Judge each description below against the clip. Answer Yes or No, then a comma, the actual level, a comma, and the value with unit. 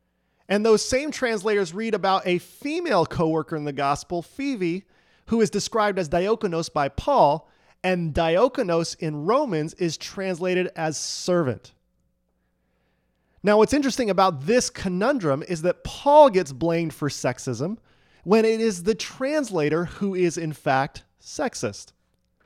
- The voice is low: No, medium, 175 Hz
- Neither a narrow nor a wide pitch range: No, wide, 6.4 semitones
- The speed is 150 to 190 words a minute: No, slow, 135 wpm